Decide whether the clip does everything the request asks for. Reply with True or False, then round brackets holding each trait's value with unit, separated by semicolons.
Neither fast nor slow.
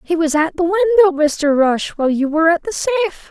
False (235 wpm)